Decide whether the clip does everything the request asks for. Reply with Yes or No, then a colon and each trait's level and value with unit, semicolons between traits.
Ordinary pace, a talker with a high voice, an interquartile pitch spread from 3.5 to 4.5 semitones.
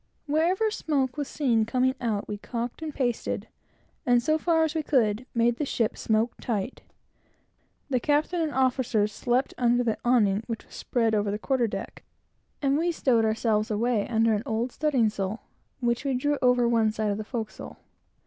Yes: average, 180 wpm; high, 240 Hz; average, 3.8 semitones